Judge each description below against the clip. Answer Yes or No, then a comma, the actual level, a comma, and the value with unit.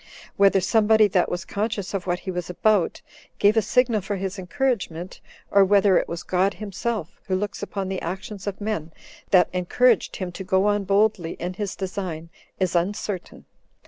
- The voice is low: No, high, 195 Hz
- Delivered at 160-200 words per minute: Yes, average, 180 wpm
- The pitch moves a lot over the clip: No, narrow, 2.5 semitones